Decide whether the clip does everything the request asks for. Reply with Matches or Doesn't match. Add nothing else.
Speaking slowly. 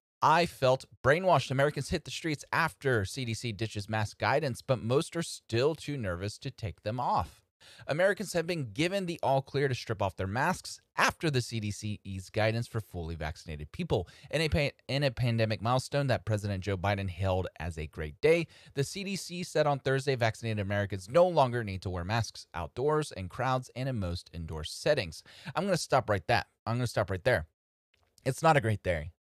Doesn't match